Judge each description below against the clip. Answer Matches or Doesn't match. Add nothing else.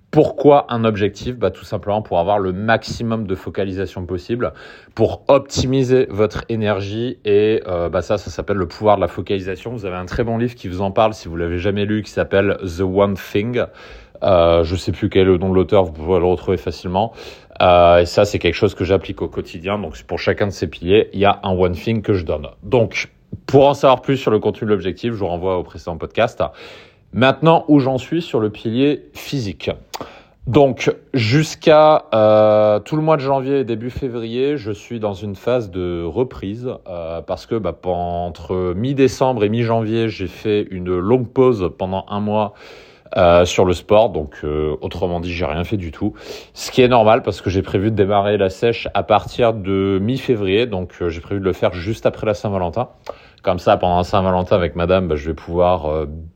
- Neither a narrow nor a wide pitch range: Matches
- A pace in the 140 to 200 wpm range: Doesn't match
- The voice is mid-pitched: Doesn't match